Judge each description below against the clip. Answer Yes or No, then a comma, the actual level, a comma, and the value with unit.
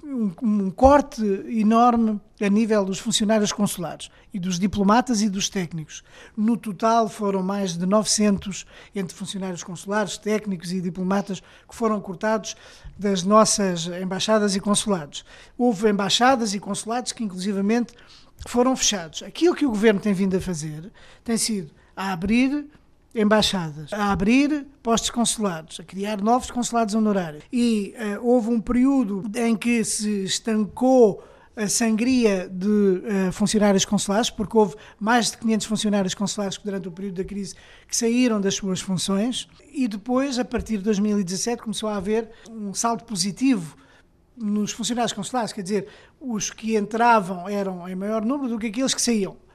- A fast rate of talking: No, average, 155 wpm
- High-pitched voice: Yes, high, 210 Hz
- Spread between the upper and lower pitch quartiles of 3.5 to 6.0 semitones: No, average, 2.8 semitones